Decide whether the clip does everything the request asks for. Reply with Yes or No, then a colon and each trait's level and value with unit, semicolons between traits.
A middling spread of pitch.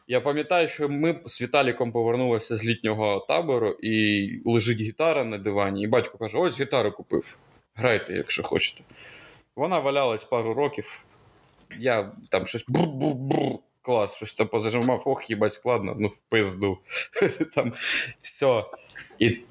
Yes: average, 4.5 semitones